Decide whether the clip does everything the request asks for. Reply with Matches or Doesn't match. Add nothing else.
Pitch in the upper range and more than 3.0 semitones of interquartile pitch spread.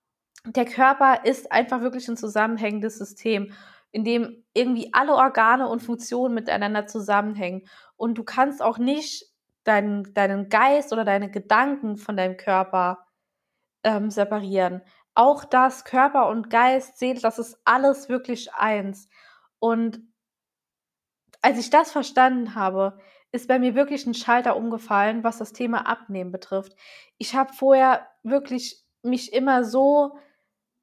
Matches